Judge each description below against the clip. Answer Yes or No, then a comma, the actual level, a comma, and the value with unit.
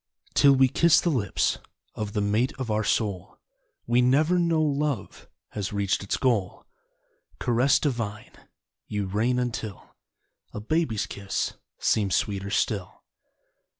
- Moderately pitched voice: No, low, 115 Hz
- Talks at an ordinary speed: No, slow, 130 wpm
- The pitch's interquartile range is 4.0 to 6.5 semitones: Yes, average, 4.7 semitones